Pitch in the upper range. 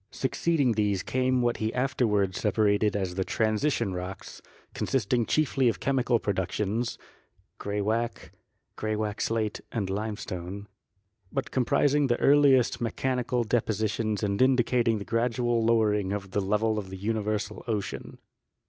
No: low, 110 Hz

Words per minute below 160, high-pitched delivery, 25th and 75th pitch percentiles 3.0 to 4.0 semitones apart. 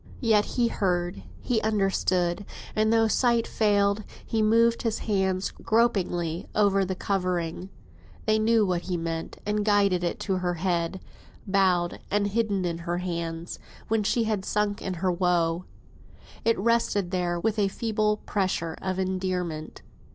Yes: average, 150 wpm; high, 195 Hz; average, 3.3 semitones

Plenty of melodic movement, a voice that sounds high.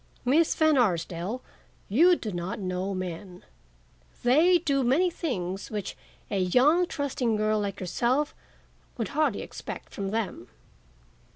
Yes: wide, 7.3 semitones; high, 225 Hz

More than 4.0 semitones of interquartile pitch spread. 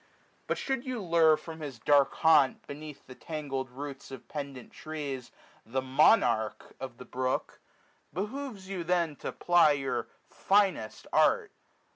Yes: average, 4.7 semitones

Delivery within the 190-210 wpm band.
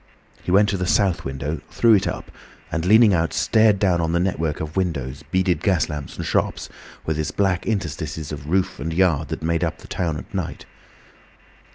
Yes: average, 200 wpm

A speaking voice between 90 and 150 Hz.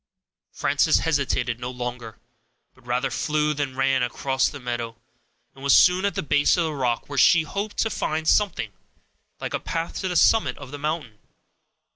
Yes: medium, 140 Hz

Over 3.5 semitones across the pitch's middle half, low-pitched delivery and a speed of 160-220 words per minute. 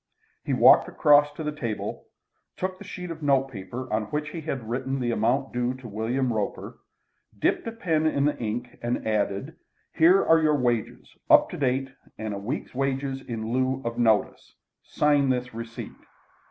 Yes: average, 4.2 semitones; low, 130 Hz; average, 175 wpm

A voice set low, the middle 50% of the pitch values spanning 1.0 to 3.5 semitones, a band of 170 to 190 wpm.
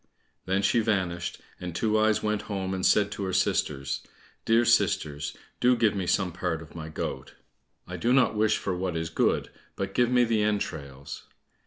No: very low, 95 Hz; average, 4.9 semitones; average, 180 wpm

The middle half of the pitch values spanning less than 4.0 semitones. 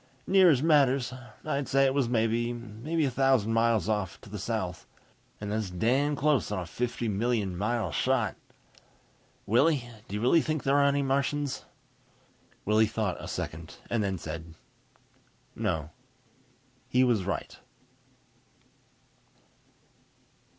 No: average, 5.0 semitones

